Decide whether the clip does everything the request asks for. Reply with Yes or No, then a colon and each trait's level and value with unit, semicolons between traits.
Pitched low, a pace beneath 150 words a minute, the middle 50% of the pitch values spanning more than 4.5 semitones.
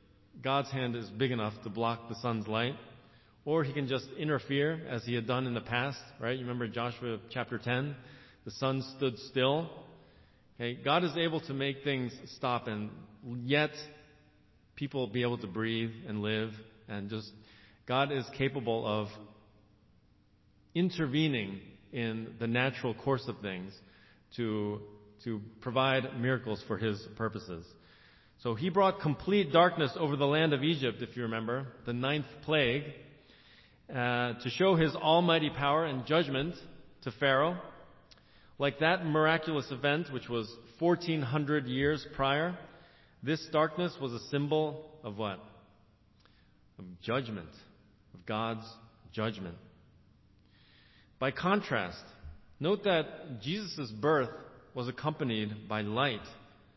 Yes: low, 120 Hz; slow, 135 wpm; average, 5.2 semitones